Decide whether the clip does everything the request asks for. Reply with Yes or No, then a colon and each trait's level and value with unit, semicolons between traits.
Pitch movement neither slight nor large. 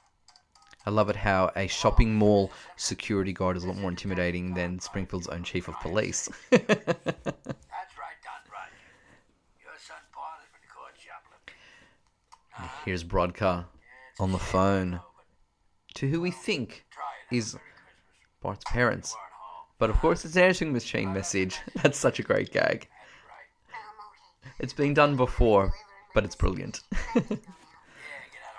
Yes: average, 4.4 semitones